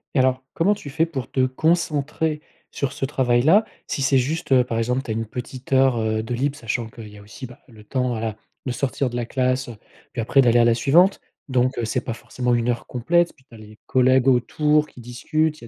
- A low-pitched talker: Yes, low, 130 Hz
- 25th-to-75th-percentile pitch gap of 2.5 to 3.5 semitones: Yes, average, 2.9 semitones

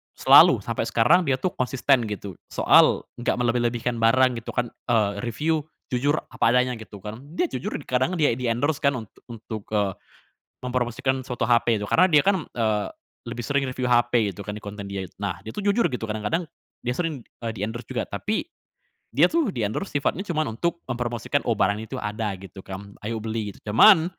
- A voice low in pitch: Yes, low, 120 Hz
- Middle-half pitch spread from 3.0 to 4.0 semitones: No, average, 4.5 semitones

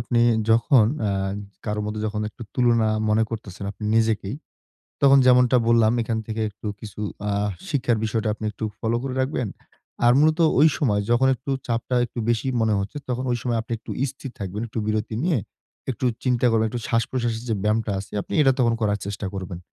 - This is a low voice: Yes, low, 115 Hz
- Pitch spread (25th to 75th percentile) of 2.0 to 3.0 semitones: Yes, average, 2.7 semitones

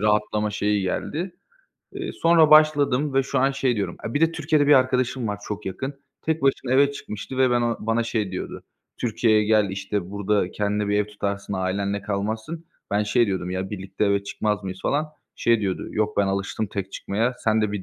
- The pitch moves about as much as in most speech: Yes, average, 4.8 semitones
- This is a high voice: No, low, 105 Hz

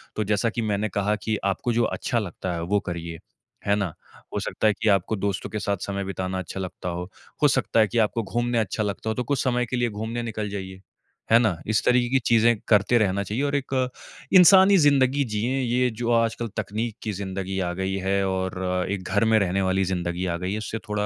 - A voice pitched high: No, low, 105 Hz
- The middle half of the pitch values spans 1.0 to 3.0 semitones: No, average, 3.6 semitones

